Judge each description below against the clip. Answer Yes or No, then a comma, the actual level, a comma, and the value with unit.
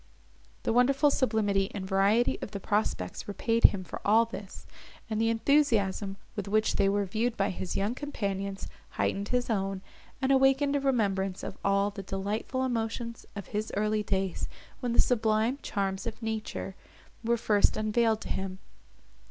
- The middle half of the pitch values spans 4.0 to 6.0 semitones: No, average, 3.1 semitones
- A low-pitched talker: No, high, 215 Hz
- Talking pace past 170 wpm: No, average, 160 wpm